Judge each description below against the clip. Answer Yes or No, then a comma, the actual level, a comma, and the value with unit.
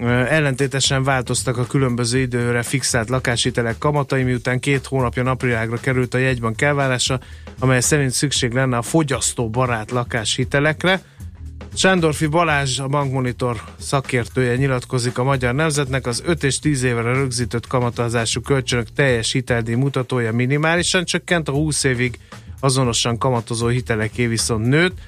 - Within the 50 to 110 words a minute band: No, average, 130 wpm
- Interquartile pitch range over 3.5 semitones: No, narrow, 2.5 semitones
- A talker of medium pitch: No, low, 130 Hz